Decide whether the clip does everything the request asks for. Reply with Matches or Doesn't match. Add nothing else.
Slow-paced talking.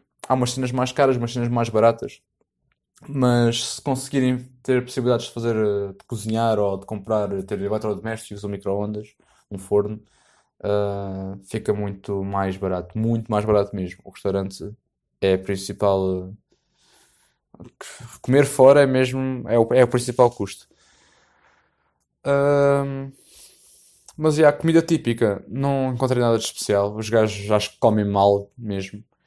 Doesn't match